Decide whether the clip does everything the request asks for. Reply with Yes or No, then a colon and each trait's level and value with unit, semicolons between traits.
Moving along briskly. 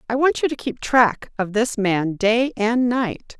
Yes: fast, 210 wpm